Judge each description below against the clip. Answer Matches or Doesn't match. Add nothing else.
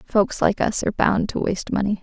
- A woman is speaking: Matches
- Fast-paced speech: Matches